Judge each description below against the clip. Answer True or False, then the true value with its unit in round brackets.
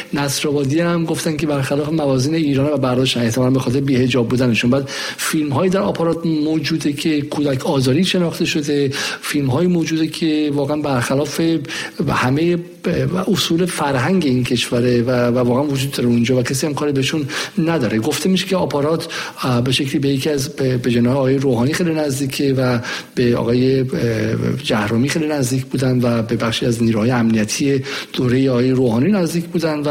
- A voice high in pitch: False (140 Hz)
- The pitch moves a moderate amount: True (4.0 semitones)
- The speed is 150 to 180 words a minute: True (155 wpm)